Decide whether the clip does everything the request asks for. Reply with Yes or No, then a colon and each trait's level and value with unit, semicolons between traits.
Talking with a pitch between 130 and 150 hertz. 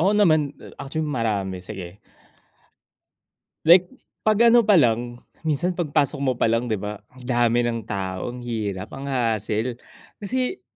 No: low, 120 Hz